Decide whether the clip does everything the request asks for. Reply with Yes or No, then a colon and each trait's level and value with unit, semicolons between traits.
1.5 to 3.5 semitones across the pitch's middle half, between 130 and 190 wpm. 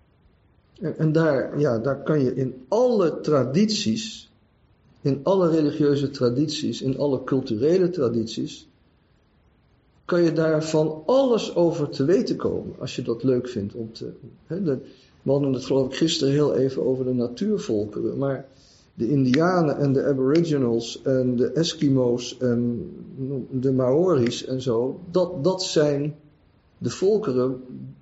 No: average, 4.2 semitones; average, 140 wpm